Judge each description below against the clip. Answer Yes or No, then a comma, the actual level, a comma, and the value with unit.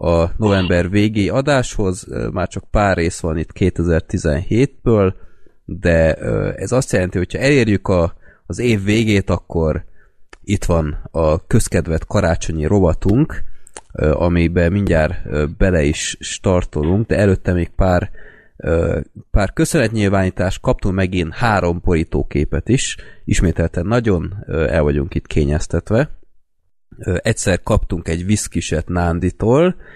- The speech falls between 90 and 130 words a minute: Yes, average, 110 wpm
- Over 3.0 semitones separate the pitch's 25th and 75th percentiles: Yes, average, 3.8 semitones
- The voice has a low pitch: Yes, very low, 90 Hz